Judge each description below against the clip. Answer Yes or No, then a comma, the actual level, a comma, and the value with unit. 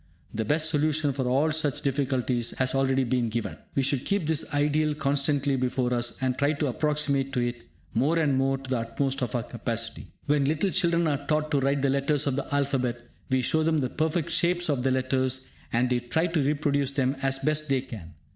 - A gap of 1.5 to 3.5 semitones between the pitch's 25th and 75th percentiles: Yes, average, 2.8 semitones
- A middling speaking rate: No, fast, 210 wpm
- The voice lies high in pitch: No, medium, 140 Hz